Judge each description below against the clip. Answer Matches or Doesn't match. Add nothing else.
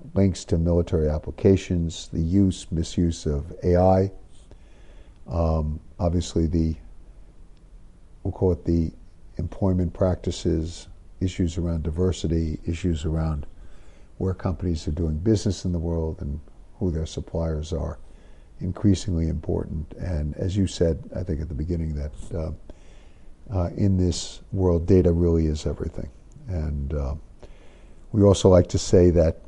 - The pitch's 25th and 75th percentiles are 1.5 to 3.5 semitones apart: Matches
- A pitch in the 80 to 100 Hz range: Matches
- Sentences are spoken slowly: Matches